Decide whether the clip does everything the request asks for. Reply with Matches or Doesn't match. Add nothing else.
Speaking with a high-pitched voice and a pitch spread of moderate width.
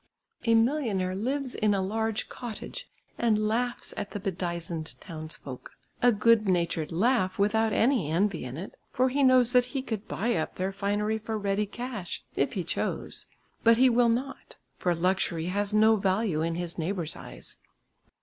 Matches